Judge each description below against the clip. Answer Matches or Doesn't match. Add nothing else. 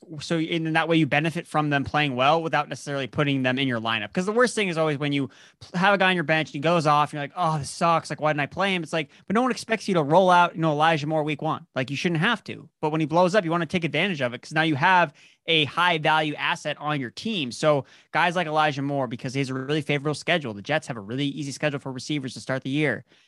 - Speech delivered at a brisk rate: Matches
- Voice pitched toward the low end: Doesn't match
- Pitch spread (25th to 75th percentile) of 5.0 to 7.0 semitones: Doesn't match